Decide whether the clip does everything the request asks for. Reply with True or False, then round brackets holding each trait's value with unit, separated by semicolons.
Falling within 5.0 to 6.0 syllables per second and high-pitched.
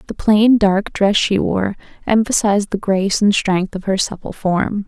False (4.6 syllables/s; 200 Hz)